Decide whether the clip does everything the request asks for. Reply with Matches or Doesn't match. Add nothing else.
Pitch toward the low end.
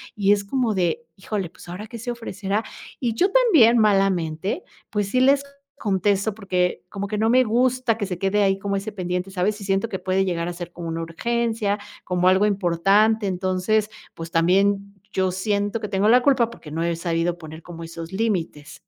Doesn't match